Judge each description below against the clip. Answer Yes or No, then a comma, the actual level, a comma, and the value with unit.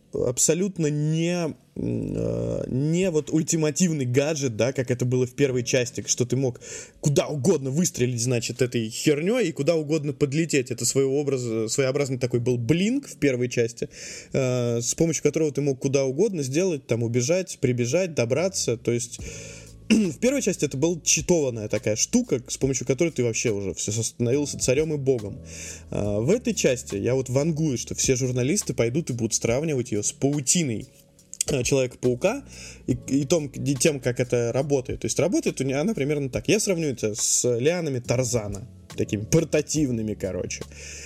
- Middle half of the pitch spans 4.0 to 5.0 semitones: Yes, average, 4.7 semitones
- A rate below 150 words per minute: No, average, 155 wpm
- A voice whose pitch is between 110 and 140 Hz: Yes, low, 135 Hz